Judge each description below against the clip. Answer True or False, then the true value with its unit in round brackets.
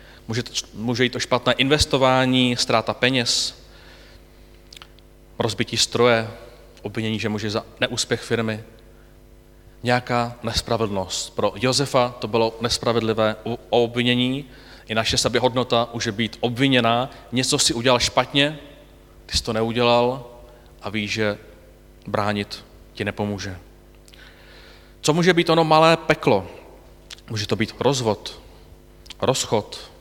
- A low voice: True (115 Hz)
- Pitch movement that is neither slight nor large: True (3.3 semitones)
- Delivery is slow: True (110 wpm)